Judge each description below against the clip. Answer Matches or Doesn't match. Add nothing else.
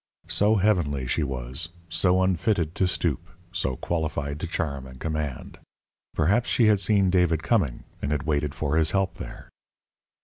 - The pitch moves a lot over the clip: Doesn't match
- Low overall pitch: Matches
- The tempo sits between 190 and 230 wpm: Doesn't match